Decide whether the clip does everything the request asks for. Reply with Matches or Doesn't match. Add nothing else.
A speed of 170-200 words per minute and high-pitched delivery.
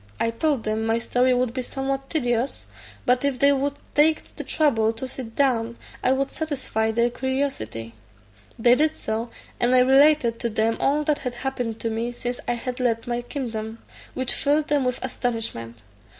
Matches